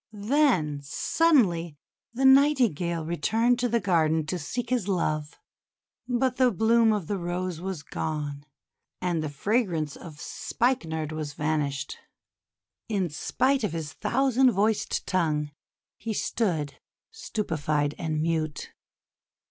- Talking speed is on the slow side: Yes, slow, 125 wpm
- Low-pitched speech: No, medium, 175 Hz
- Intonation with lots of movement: Yes, wide, 7.1 semitones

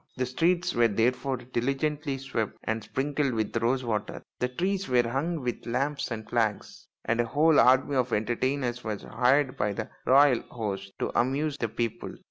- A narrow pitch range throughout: No, average, 3.2 semitones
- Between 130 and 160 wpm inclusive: No, average, 170 wpm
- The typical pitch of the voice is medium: No, low, 125 Hz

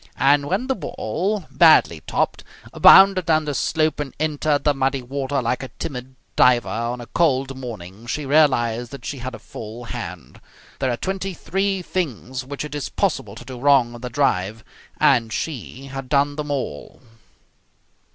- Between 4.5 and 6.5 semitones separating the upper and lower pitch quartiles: No, average, 3.9 semitones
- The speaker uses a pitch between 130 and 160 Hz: Yes, low, 135 Hz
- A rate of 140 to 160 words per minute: No, average, 170 wpm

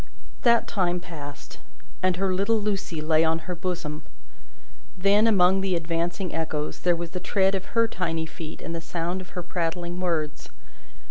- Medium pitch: Yes, medium, 175 Hz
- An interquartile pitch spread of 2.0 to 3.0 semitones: Yes, narrow, 2.6 semitones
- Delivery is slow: No, average, 165 wpm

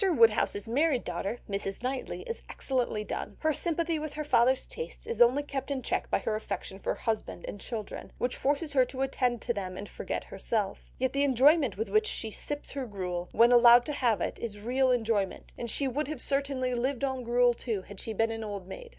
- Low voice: No, high, 245 Hz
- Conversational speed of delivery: No, fast, 215 wpm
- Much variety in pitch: No, average, 4.1 semitones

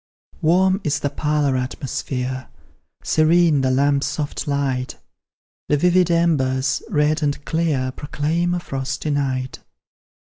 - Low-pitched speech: No, medium, 145 Hz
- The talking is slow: Yes, slow, 115 wpm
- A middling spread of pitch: Yes, average, 3.4 semitones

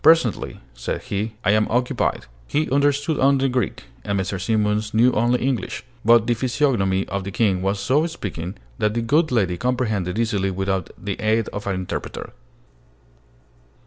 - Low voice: Yes, low, 110 Hz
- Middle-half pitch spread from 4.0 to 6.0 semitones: Yes, average, 4.5 semitones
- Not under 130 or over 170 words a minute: Yes, average, 160 wpm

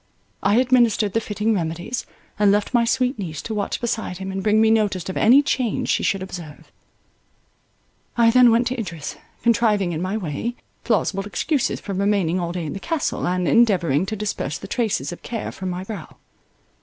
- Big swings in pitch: No, average, 4.1 semitones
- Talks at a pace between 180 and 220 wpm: Yes, average, 190 wpm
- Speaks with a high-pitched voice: Yes, high, 205 Hz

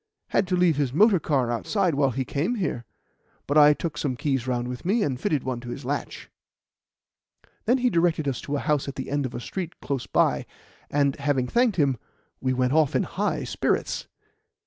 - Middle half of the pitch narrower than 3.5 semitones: No, average, 4.5 semitones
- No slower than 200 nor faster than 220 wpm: Yes, fast, 205 wpm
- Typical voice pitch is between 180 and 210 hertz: No, medium, 145 Hz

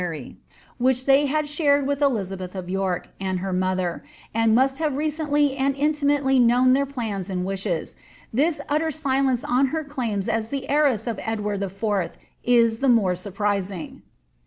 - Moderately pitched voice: No, high, 240 Hz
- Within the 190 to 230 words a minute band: No, average, 165 wpm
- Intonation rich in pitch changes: Yes, wide, 6.3 semitones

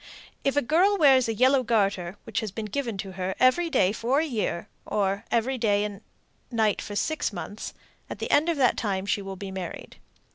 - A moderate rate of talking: No, fast, 210 wpm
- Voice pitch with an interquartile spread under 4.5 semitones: No, average, 5.0 semitones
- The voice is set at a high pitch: Yes, high, 220 Hz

